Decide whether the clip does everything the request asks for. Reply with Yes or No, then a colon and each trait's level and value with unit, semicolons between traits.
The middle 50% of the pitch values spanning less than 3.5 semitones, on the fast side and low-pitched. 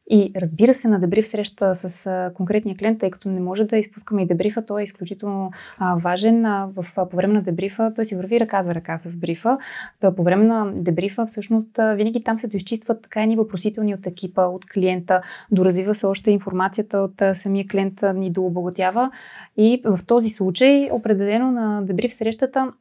No: average, 3.0 semitones; fast, 175 wpm; high, 200 Hz